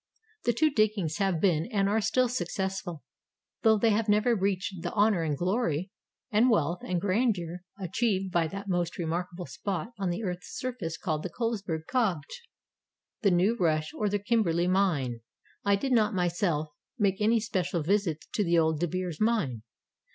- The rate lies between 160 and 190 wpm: Yes, average, 170 wpm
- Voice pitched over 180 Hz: Yes, high, 190 Hz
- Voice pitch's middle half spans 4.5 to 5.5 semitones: No, average, 3.9 semitones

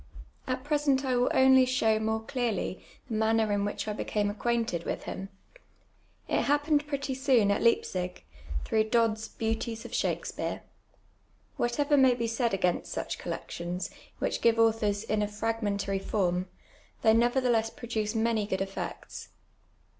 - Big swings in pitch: No, average, 3.2 semitones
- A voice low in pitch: No, high, 225 Hz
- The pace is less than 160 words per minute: Yes, average, 145 wpm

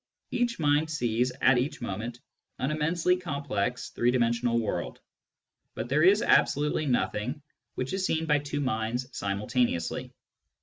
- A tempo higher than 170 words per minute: No, slow, 135 wpm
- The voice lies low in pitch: Yes, low, 130 Hz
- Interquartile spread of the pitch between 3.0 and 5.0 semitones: Yes, average, 4.4 semitones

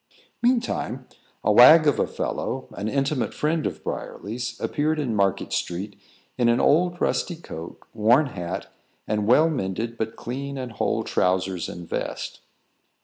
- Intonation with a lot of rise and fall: Yes, wide, 6.5 semitones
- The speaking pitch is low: Yes, low, 120 Hz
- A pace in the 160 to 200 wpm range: No, average, 145 wpm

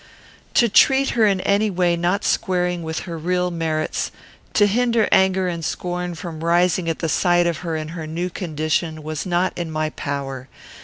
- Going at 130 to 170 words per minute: No, average, 185 wpm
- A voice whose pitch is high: No, medium, 175 Hz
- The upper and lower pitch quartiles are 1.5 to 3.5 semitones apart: Yes, narrow, 2.6 semitones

